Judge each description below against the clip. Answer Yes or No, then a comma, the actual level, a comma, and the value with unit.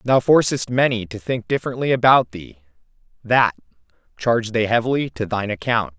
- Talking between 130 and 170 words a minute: Yes, average, 150 wpm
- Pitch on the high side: No, low, 110 Hz